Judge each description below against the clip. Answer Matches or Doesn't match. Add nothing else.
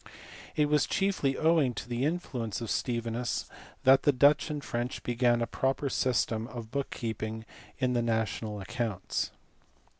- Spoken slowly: Doesn't match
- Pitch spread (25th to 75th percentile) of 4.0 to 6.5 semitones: Doesn't match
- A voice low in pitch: Matches